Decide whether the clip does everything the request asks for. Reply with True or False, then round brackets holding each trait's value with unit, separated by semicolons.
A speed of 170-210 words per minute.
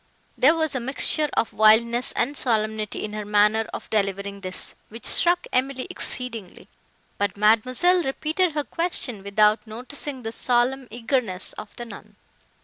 False (145 wpm)